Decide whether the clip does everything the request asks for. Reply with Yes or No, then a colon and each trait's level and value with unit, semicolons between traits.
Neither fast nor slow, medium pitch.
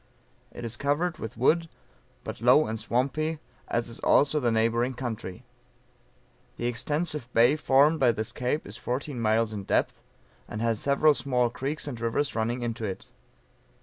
No: average, 160 wpm; low, 120 Hz